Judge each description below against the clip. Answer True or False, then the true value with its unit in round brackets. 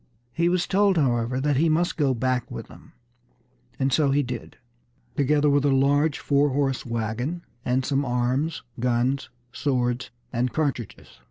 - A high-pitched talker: False (135 Hz)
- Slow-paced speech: False (155 wpm)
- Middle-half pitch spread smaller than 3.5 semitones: True (3.0 semitones)